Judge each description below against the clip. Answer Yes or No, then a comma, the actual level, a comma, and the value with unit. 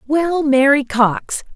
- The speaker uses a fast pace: No, slow, 115 wpm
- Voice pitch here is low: No, very high, 280 Hz